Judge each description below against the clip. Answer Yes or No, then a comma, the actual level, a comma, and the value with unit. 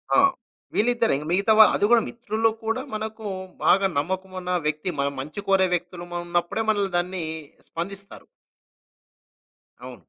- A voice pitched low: No, high, 190 Hz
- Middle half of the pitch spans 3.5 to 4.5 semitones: Yes, average, 3.8 semitones